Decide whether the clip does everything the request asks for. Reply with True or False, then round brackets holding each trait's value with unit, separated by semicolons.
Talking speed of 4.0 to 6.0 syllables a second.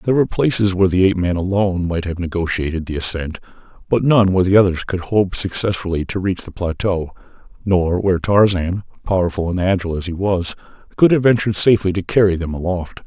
False (6.3 syllables/s)